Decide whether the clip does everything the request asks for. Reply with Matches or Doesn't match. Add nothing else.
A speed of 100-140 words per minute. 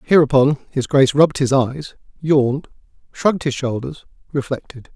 Matches